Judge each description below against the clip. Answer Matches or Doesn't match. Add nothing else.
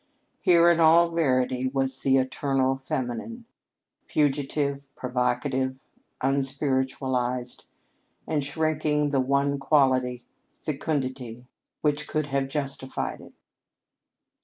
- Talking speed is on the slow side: Matches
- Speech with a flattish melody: Matches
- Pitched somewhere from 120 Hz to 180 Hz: Matches